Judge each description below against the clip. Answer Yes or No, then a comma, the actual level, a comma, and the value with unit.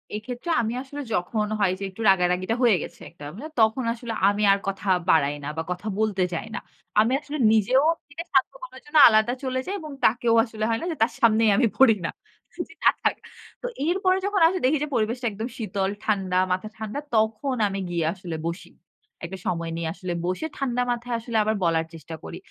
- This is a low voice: No, high, 220 Hz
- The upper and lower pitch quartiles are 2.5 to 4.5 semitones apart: No, average, 5.0 semitones